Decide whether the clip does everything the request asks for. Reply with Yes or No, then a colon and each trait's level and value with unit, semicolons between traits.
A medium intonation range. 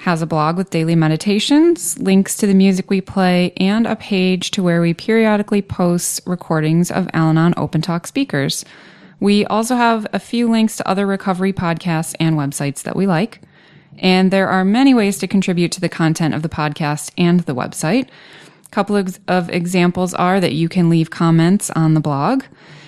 Yes: average, 3.4 semitones